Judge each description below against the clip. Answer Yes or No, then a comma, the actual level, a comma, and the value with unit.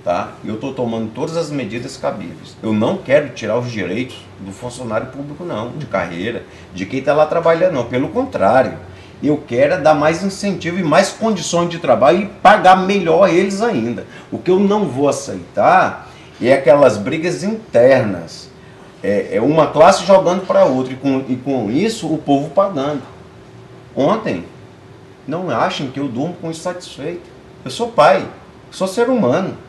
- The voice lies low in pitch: No, medium, 160 Hz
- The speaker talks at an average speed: Yes, average, 160 wpm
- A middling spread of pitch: No, wide, 6.3 semitones